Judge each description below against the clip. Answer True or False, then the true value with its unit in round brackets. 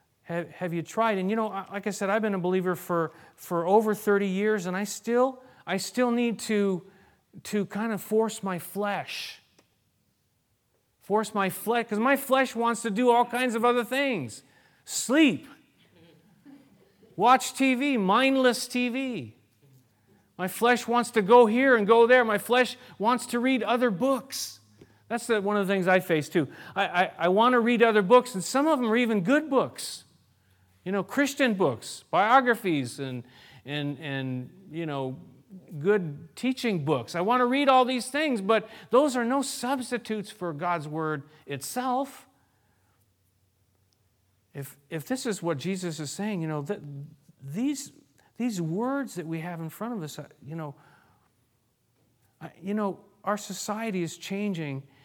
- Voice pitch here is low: False (205 Hz)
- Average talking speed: True (165 wpm)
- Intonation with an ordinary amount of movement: False (6.9 semitones)